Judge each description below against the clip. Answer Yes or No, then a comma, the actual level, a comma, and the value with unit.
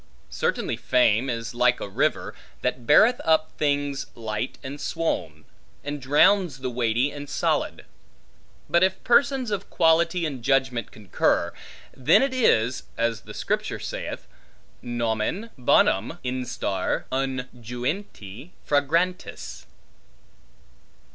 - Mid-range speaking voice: No, low, 130 Hz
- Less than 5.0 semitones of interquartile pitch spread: No, wide, 5.5 semitones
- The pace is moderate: No, slow, 110 wpm